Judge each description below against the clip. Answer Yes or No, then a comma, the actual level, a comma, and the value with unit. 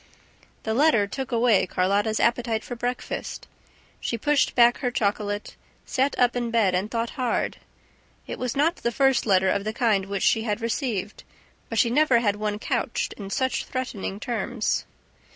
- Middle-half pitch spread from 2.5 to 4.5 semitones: Yes, average, 3.1 semitones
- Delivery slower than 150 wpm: No, average, 170 wpm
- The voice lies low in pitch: No, high, 230 Hz